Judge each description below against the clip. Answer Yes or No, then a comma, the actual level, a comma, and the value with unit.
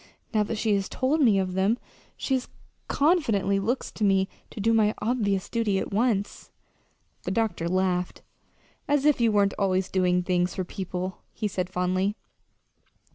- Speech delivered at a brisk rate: No, average, 160 wpm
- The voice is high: Yes, high, 200 Hz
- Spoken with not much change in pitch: No, average, 3.4 semitones